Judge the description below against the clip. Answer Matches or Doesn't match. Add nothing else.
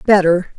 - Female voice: Matches